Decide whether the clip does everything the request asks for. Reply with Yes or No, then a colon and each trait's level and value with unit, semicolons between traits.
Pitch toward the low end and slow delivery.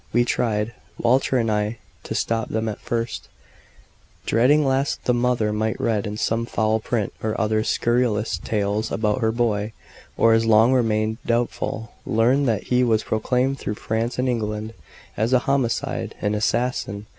No: low, 115 Hz; average, 160 wpm